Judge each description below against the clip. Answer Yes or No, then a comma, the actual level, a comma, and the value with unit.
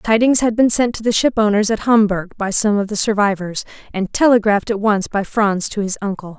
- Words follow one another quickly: Yes, fast, 215 wpm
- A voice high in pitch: Yes, high, 210 Hz